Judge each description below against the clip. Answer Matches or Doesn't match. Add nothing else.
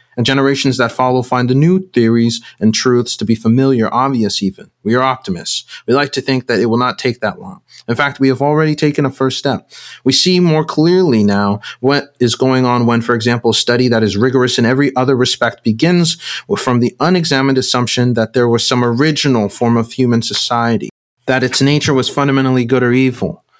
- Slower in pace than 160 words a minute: Doesn't match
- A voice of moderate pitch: Doesn't match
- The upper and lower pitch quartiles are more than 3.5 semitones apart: Doesn't match